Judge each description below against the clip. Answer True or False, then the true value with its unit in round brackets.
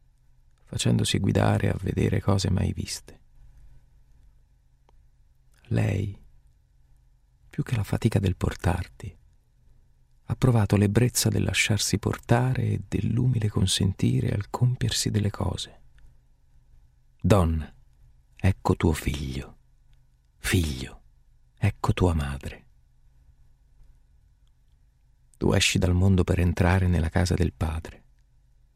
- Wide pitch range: True (7.8 semitones)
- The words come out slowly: True (95 wpm)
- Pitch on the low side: True (90 Hz)